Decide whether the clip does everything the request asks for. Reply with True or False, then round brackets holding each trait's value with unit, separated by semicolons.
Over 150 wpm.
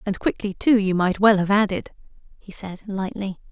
True (190 wpm)